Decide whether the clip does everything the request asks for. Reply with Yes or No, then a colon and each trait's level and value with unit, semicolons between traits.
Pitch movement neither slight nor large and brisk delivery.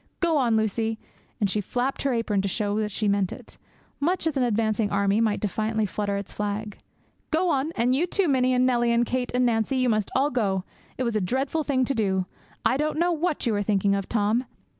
Yes: average, 4.2 semitones; fast, 225 wpm